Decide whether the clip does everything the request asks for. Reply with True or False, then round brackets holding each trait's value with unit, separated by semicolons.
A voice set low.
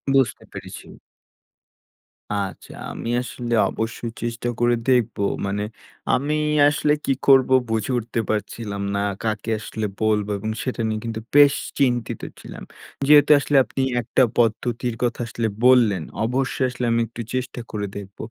True (120 Hz)